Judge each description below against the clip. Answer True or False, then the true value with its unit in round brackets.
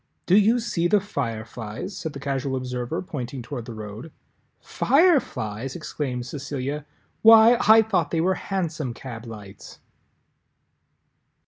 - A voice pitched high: False (140 Hz)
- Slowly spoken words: True (125 wpm)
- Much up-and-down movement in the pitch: True (7.7 semitones)